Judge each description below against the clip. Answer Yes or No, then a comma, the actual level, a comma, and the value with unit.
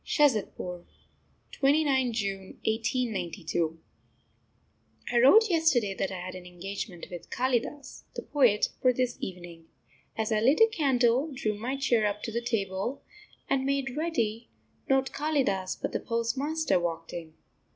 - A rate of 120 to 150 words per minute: Yes, average, 140 wpm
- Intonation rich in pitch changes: Yes, wide, 6.0 semitones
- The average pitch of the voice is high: Yes, high, 235 Hz